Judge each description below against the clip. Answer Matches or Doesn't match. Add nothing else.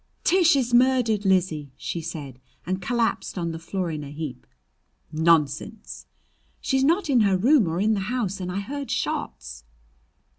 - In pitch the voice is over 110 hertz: Matches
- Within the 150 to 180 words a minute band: Matches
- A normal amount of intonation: Doesn't match